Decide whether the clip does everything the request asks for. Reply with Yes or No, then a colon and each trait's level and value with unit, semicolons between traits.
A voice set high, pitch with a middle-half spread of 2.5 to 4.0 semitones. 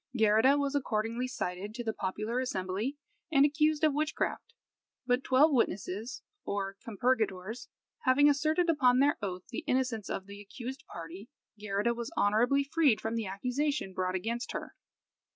No: high, 235 Hz; average, 5.2 semitones